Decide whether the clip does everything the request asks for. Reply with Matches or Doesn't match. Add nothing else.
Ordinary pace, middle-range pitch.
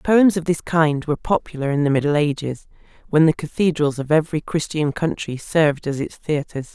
Matches